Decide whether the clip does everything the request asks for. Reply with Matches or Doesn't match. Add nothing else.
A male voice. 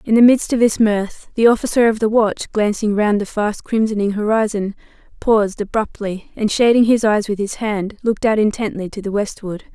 Doesn't match